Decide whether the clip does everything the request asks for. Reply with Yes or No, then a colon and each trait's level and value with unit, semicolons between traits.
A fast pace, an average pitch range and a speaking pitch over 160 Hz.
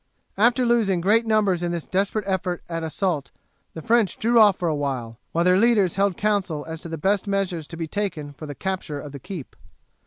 Yes: fast, 215 wpm; average, 4.1 semitones; medium, 185 Hz